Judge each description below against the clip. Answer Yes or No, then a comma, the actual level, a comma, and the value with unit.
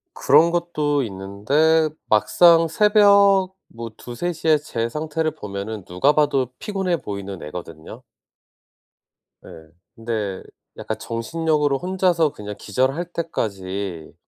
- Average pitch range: No, wide, 8.2 semitones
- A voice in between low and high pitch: Yes, medium, 145 Hz